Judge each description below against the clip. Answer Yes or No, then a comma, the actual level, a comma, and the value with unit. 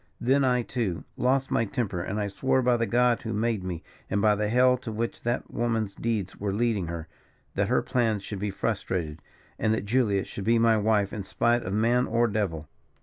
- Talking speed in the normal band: No, fast, 210 wpm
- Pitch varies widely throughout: No, average, 3.2 semitones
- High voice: No, low, 110 Hz